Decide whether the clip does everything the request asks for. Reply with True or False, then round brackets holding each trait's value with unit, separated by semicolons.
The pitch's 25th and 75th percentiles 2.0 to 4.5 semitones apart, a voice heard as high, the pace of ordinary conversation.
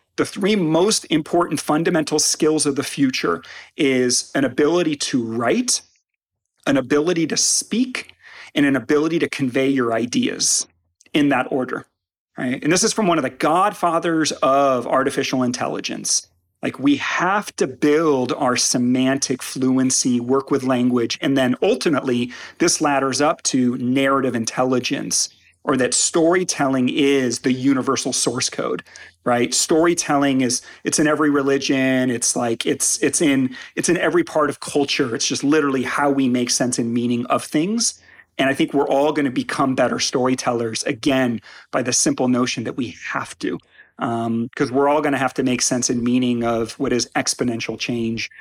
False (3.4 semitones; 135 Hz; 165 wpm)